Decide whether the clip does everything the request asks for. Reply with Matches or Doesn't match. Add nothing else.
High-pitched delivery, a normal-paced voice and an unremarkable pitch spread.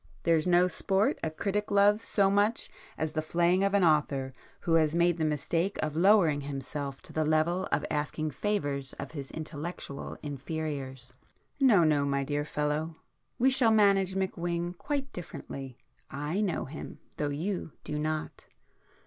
Doesn't match